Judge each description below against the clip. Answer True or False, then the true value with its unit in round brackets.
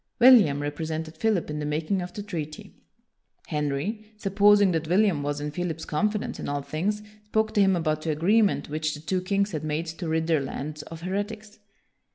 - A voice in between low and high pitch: True (165 Hz)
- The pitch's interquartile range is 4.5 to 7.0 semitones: True (5.0 semitones)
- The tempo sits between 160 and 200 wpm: True (190 wpm)